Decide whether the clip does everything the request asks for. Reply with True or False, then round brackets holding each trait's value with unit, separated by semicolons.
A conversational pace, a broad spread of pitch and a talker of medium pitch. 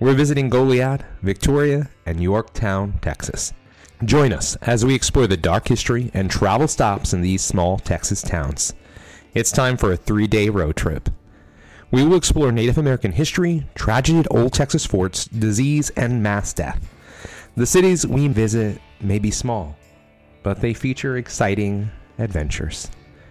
False (150 wpm; 5.9 semitones; 110 Hz)